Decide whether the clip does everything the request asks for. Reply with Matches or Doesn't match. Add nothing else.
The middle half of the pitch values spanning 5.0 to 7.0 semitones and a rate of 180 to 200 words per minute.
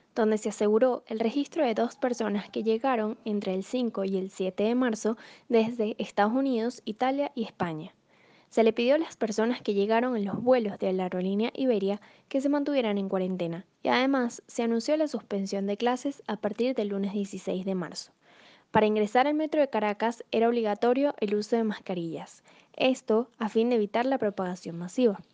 Doesn't match